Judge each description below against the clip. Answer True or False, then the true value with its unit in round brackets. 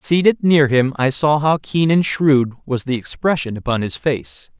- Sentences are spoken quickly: False (195 wpm)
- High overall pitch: False (145 Hz)